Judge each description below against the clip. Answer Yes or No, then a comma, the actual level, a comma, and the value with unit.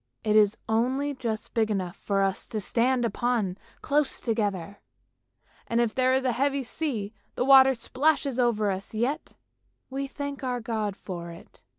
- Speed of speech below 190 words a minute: Yes, average, 165 wpm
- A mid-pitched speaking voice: No, high, 235 Hz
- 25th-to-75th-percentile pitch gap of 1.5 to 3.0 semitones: No, average, 4.0 semitones